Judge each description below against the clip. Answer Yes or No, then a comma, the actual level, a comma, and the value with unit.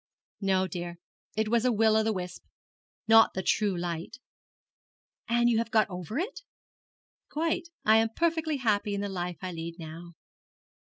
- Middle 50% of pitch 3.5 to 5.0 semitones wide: Yes, average, 4.5 semitones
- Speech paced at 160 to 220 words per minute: Yes, average, 165 wpm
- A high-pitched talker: Yes, high, 210 Hz